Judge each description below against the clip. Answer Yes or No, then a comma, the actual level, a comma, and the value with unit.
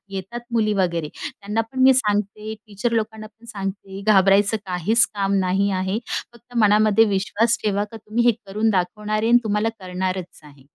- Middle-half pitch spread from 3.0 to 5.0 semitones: No, narrow, 2.5 semitones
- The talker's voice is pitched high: Yes, high, 210 Hz